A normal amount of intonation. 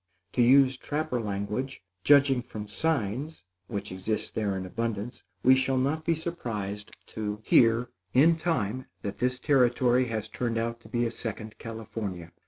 Yes: average, 3.8 semitones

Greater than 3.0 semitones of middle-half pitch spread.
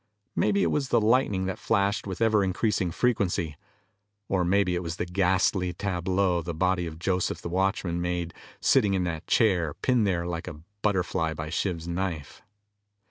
No: narrow, 2.5 semitones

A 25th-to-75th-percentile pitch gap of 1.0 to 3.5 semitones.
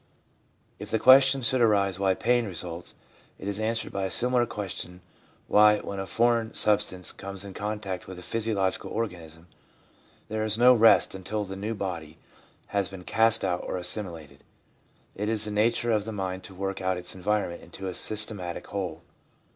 Yes: average, 3.0 semitones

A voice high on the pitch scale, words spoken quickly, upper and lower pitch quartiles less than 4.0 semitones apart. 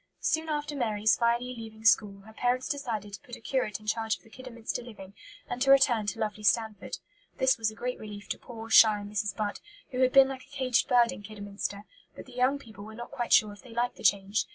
Yes: high, 225 Hz; fast, 235 wpm; average, 3.1 semitones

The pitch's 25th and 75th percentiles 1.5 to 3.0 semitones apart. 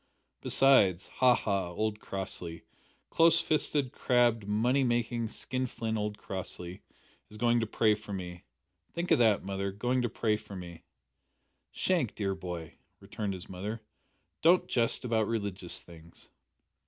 No: average, 4.0 semitones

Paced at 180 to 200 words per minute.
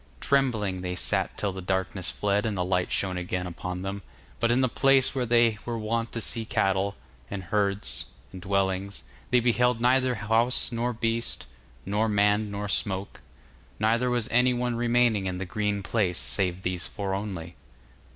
No: average, 170 wpm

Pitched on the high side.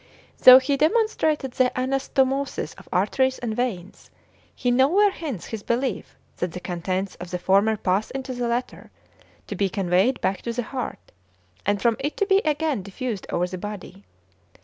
Yes: high, 240 Hz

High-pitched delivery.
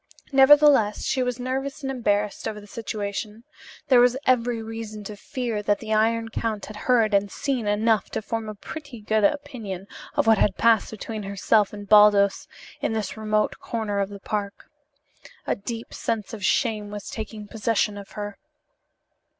Yes: high, 215 Hz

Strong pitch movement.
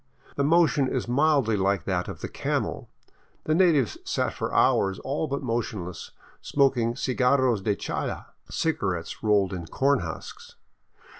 Yes: wide, 6.1 semitones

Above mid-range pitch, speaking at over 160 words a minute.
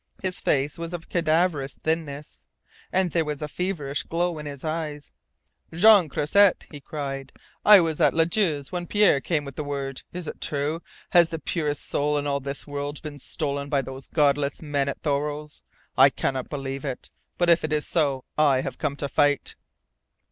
No: medium, 150 Hz; average, 185 wpm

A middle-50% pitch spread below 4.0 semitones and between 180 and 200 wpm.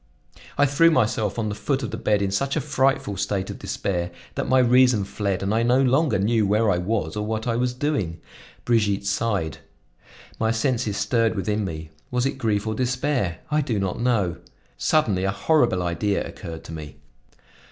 No: average, 4.3 semitones; average, 190 wpm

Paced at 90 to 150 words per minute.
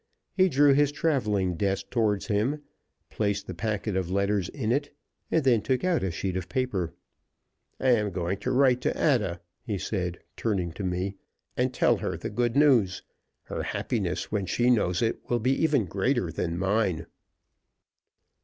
No: average, 170 wpm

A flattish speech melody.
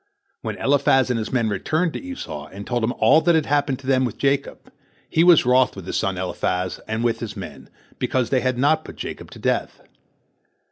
No: average, 4.5 semitones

